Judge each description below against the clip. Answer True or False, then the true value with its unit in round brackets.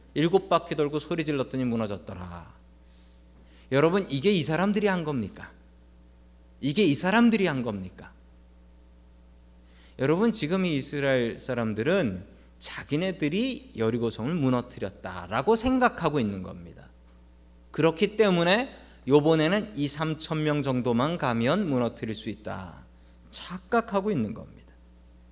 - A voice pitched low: True (120 Hz)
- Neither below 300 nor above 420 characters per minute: False (275 characters per minute)